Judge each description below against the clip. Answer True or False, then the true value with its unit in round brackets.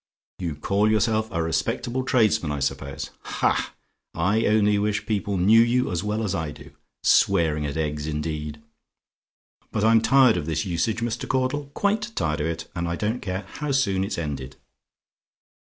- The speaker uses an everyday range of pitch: False (5.9 semitones)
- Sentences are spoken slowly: False (170 wpm)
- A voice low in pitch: True (100 Hz)